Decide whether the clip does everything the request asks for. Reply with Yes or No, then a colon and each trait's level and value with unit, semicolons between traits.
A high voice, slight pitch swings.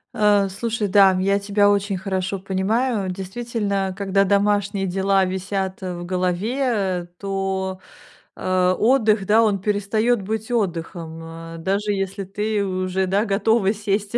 Yes: high, 195 Hz; narrow, 1.7 semitones